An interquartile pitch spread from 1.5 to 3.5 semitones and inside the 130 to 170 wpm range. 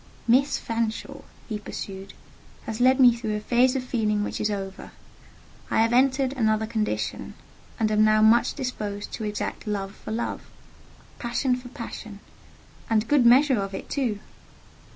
Yes: average, 2.9 semitones; average, 150 wpm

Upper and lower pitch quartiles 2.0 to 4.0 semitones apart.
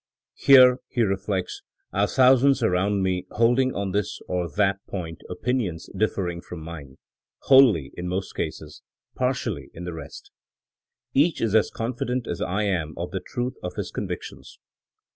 No: wide, 5.5 semitones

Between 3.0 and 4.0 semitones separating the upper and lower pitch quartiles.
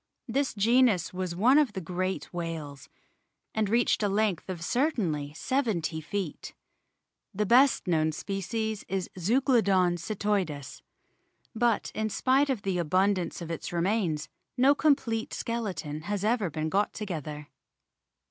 No: average, 5.1 semitones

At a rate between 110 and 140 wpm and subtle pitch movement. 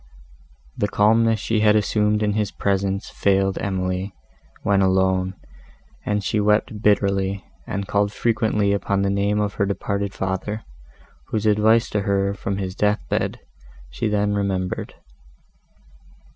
Yes: slow, 135 wpm; narrow, 1.3 semitones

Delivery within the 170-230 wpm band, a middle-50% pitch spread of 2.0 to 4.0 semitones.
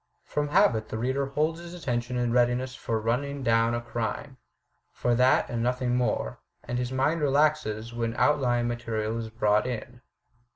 Yes: average, 175 wpm; average, 2.7 semitones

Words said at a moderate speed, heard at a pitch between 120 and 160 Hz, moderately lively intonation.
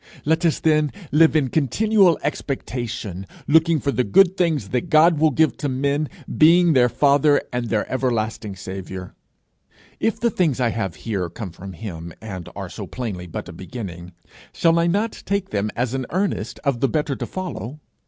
No: average, 180 wpm; low, 135 Hz; wide, 6.9 semitones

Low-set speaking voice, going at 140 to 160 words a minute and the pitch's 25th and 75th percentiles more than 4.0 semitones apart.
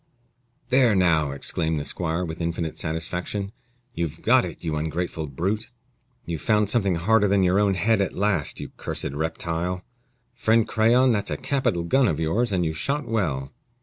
No: very low, 90 Hz; average, 170 wpm; average, 4.6 semitones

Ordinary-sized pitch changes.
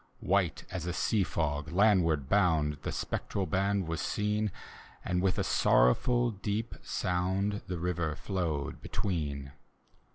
Yes: average, 4.1 semitones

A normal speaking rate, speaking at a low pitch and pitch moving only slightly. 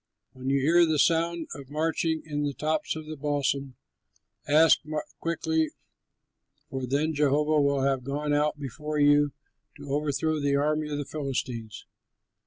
No: average, 150 wpm; medium, 145 Hz; narrow, 1.9 semitones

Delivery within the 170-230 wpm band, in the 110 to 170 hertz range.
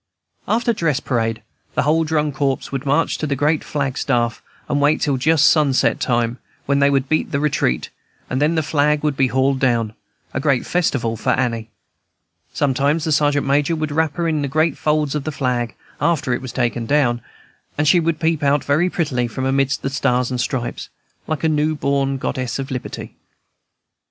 Yes: average, 195 wpm; medium, 140 Hz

